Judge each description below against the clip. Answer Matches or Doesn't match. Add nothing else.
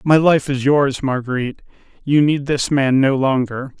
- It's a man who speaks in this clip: Matches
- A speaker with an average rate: Matches